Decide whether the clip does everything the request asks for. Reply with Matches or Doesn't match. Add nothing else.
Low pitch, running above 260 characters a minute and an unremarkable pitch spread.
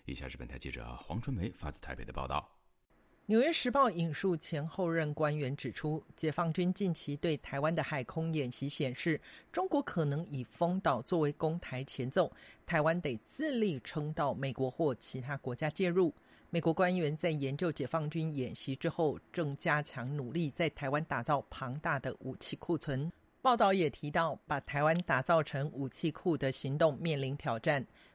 Doesn't match